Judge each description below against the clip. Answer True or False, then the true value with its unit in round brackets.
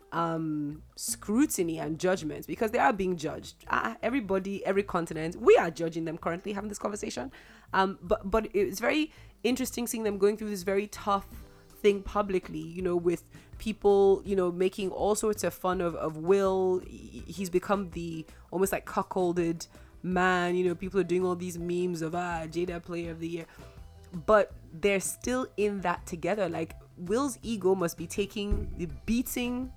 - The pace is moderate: True (175 wpm)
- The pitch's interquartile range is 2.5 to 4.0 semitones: True (3.2 semitones)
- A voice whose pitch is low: False (185 Hz)